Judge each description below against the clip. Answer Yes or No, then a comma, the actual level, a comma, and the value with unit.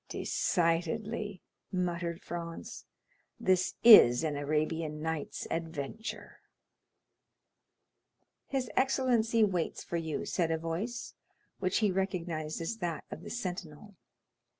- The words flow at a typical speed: No, slow, 105 wpm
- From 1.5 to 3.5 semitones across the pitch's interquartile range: No, average, 4.4 semitones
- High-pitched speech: No, medium, 175 Hz